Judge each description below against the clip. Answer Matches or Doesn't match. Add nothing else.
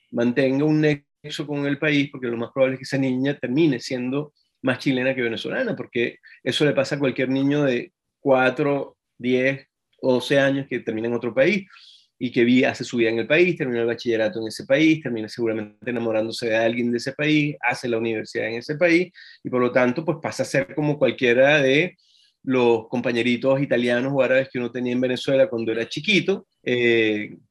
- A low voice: Matches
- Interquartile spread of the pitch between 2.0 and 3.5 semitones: Matches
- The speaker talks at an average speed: Doesn't match